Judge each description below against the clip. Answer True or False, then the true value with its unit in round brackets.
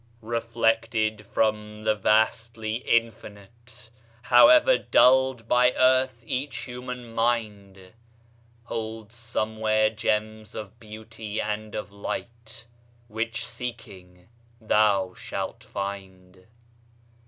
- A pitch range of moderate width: False (1.7 semitones)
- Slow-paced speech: True (85 wpm)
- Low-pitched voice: True (110 Hz)